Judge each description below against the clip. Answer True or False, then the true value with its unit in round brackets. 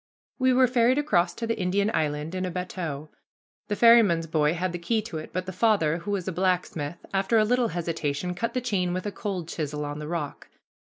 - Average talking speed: False (220 wpm)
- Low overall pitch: False (180 Hz)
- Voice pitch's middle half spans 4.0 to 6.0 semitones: True (4.7 semitones)